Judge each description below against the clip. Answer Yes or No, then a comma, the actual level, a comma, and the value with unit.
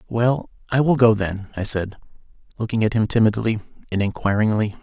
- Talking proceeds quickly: No, average, 160 wpm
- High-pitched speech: No, low, 110 Hz